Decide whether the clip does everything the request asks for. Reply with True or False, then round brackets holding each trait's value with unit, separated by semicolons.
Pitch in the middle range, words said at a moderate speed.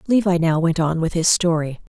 False (170 Hz; 215 wpm)